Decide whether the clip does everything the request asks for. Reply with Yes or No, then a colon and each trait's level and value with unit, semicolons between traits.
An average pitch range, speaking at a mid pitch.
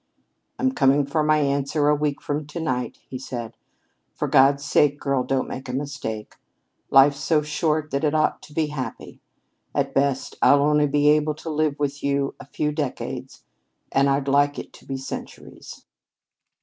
No: narrow, 1.7 semitones; medium, 145 Hz